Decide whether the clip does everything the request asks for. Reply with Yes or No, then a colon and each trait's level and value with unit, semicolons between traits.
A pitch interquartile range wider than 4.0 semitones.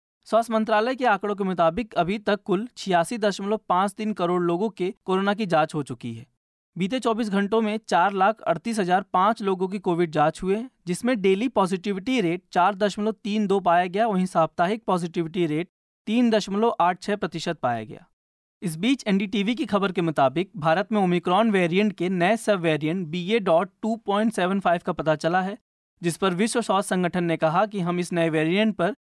No: average, 3.7 semitones